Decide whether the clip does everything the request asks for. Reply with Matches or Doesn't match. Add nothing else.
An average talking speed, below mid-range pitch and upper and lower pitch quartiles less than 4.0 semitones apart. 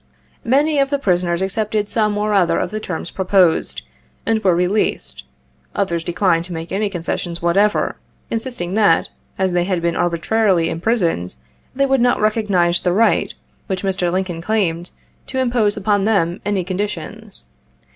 Doesn't match